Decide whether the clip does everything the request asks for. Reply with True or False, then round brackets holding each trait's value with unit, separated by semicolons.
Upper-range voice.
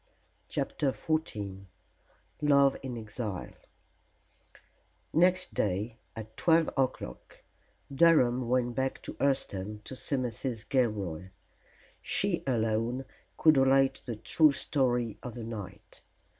False (125 Hz)